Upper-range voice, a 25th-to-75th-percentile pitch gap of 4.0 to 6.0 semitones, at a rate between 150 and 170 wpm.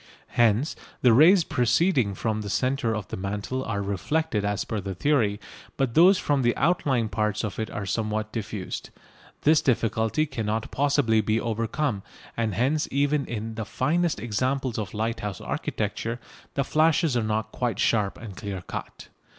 No: low, 115 Hz; average, 4.6 semitones; average, 160 wpm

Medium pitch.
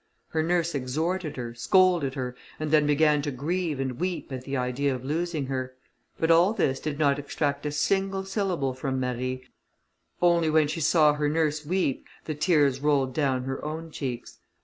Yes: medium, 150 Hz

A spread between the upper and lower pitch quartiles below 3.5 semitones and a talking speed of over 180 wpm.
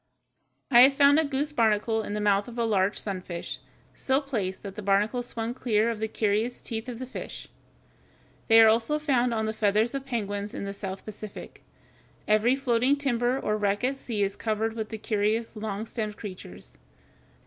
Yes: average, 2.9 semitones; average, 190 wpm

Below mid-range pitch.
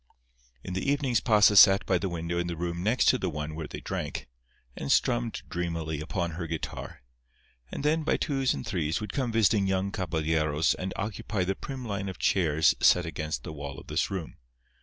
Yes: very low, 90 Hz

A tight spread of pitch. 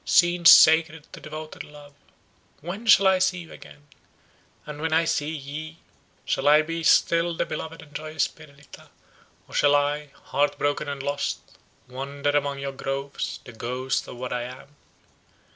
Yes: narrow, 2.3 semitones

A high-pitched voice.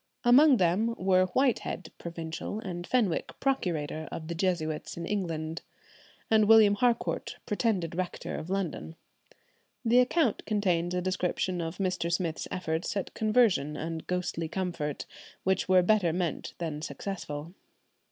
No: medium, 180 Hz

